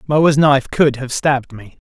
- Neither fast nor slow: Yes, average, 195 wpm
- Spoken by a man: Yes, male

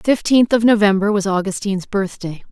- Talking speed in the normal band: Yes, average, 165 wpm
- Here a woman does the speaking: Yes, female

